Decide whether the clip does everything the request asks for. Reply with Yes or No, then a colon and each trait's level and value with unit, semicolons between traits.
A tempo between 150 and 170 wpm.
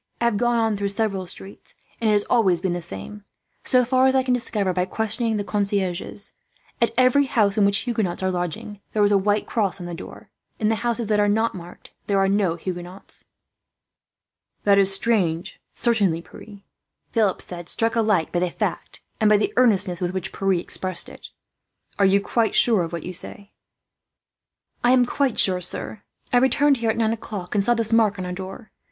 No: fast, 205 wpm